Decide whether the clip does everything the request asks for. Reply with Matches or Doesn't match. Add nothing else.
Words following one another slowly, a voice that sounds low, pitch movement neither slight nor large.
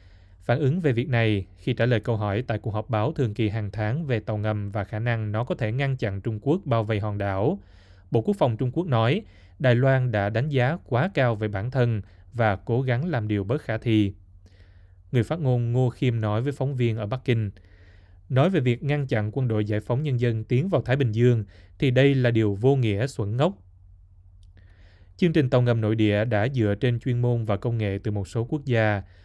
Doesn't match